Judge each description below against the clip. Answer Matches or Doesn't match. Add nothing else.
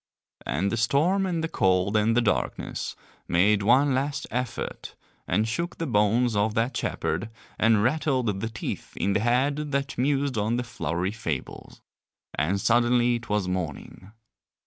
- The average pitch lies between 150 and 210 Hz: Doesn't match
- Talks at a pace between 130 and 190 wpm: Matches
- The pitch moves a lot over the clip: Doesn't match